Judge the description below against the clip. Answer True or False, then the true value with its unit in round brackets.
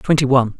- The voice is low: True (130 Hz)